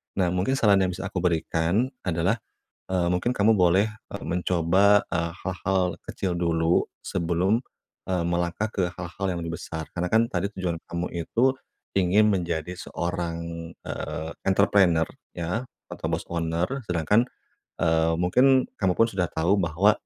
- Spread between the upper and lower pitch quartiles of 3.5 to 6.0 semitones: No, average, 2.8 semitones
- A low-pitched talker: Yes, very low, 90 Hz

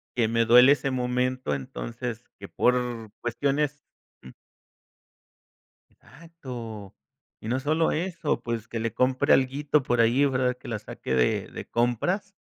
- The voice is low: Yes, low, 125 Hz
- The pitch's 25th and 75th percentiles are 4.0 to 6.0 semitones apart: No, average, 3.2 semitones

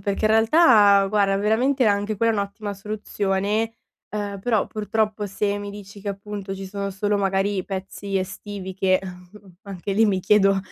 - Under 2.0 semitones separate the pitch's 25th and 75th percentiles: Yes, narrow, 1.3 semitones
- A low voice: No, high, 205 Hz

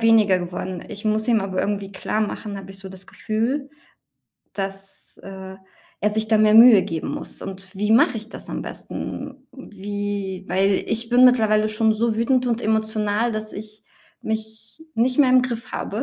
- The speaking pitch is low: No, high, 215 Hz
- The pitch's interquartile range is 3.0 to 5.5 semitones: No, narrow, 2.5 semitones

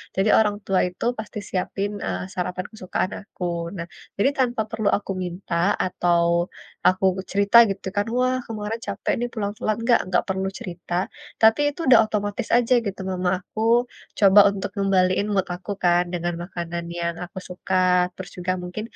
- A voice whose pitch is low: No, high, 195 Hz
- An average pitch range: Yes, average, 3.0 semitones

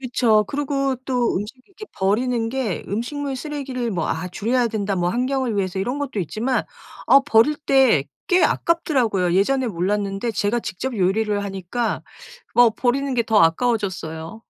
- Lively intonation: No, average, 5.0 semitones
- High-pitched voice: Yes, high, 230 Hz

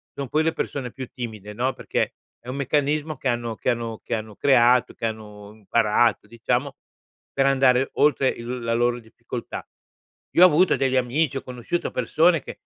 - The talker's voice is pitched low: Yes, low, 125 Hz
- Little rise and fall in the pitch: No, average, 3.0 semitones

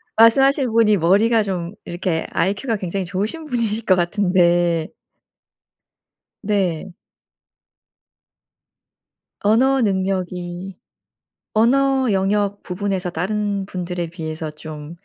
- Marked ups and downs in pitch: No, average, 3.8 semitones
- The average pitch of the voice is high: Yes, high, 195 Hz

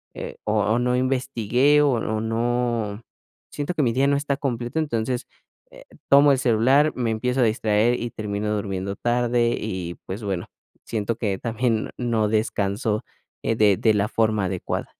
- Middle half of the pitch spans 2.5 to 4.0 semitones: Yes, average, 2.8 semitones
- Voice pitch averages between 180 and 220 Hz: No, low, 115 Hz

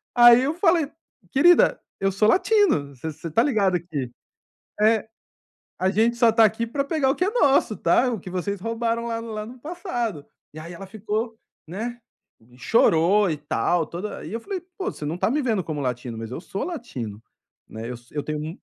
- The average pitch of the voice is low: No, high, 215 Hz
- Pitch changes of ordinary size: No, wide, 6.9 semitones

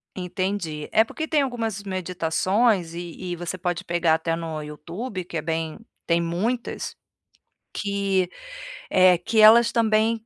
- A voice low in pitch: No, medium, 185 Hz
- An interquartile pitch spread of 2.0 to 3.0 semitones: No, average, 4.4 semitones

